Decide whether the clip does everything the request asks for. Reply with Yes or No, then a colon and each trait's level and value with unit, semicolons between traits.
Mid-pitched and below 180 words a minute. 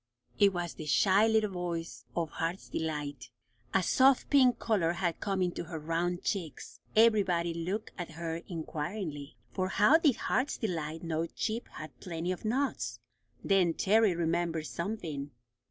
Yes: medium, 175 Hz; average, 150 wpm